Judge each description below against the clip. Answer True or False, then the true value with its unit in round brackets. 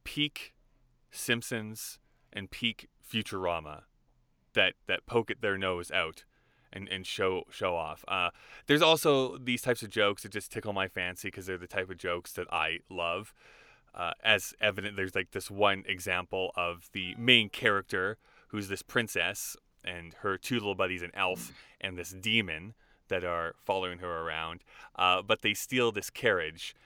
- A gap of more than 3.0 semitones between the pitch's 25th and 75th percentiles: True (3.6 semitones)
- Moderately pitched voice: False (95 Hz)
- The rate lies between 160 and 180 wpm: True (165 wpm)